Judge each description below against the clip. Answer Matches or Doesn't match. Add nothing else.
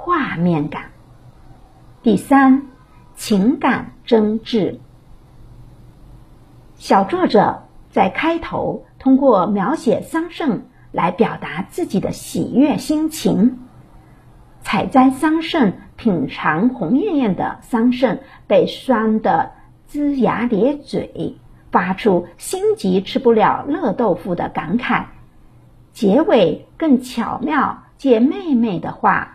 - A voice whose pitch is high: Matches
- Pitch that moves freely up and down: Doesn't match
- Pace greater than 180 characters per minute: Doesn't match